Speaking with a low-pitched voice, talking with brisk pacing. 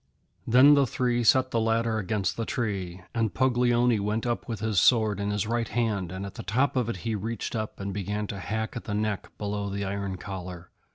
Yes: low, 110 Hz; fast, 220 wpm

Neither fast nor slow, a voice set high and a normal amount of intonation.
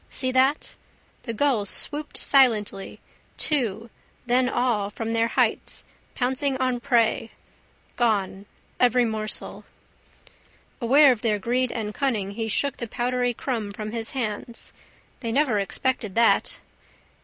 No: slow, 125 wpm; high, 235 Hz; average, 3.2 semitones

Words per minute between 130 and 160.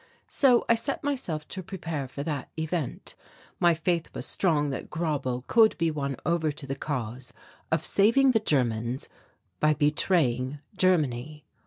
Yes: average, 150 wpm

